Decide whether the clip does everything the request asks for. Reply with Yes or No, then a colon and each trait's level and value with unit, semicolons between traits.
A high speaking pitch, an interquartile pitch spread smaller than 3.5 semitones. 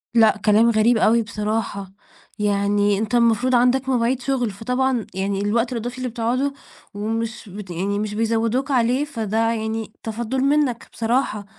Yes: high, 225 Hz; average, 2.8 semitones